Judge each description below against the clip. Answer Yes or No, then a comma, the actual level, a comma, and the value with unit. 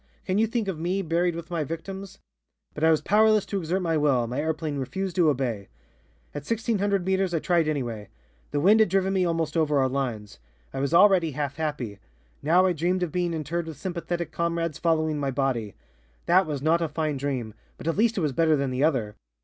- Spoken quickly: Yes, fast, 215 wpm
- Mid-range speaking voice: Yes, medium, 160 Hz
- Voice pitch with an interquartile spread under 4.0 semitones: No, average, 4.3 semitones